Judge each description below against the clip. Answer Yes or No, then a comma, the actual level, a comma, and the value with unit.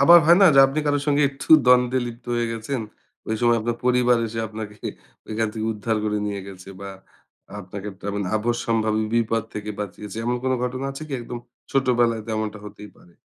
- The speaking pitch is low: Yes, low, 115 Hz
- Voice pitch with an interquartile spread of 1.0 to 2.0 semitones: No, average, 2.9 semitones